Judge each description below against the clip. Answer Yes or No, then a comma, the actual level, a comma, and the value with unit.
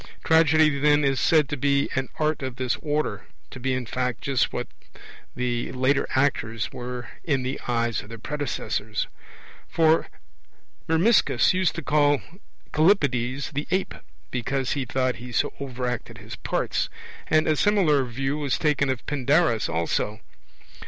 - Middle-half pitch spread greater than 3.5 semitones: No, average, 3.2 semitones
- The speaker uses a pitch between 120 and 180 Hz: Yes, low, 135 Hz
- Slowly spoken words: No, average, 150 wpm